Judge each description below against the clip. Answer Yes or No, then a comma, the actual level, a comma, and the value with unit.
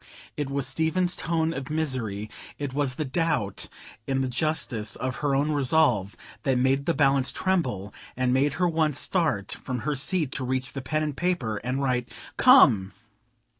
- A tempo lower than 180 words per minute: Yes, average, 170 wpm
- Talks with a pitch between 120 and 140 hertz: Yes, low, 135 Hz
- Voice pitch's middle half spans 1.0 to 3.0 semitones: No, average, 3.8 semitones